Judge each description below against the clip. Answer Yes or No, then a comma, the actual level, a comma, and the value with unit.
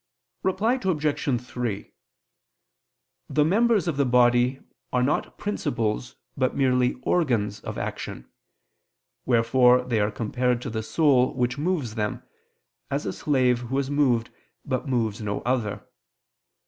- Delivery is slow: Yes, slow, 130 wpm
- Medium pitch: No, low, 125 Hz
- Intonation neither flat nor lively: Yes, average, 3.3 semitones